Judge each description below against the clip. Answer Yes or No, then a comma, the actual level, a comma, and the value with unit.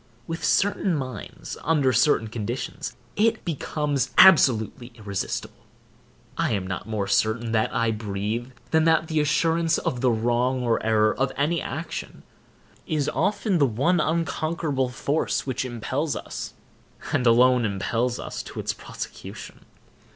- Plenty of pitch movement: Yes, wide, 5.8 semitones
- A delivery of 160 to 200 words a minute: No, slow, 135 wpm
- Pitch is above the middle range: No, low, 130 Hz